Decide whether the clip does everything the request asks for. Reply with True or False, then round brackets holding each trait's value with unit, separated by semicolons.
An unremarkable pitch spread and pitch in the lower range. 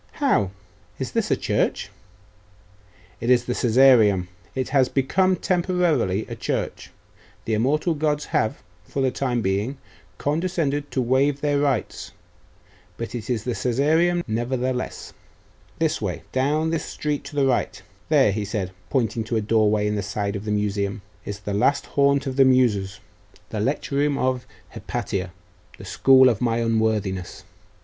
True (5.0 semitones; 125 Hz)